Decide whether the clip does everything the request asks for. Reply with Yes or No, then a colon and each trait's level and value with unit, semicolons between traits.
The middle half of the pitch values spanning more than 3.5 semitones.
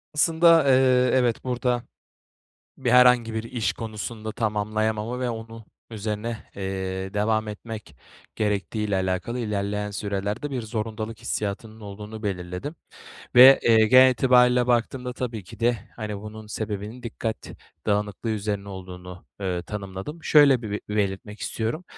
No: average, 3.0 semitones